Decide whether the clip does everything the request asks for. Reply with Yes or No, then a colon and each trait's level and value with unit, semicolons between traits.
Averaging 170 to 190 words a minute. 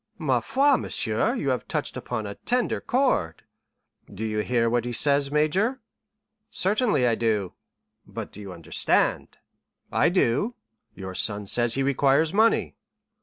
No: average, 145 wpm